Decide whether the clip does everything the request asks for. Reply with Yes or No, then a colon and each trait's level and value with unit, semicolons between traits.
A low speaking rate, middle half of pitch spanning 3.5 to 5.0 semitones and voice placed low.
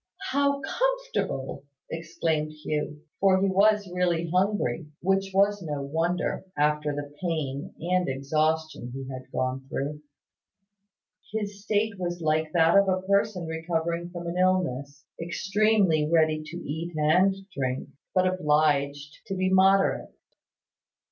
No: slow, 130 wpm; average, 4.1 semitones; medium, 170 Hz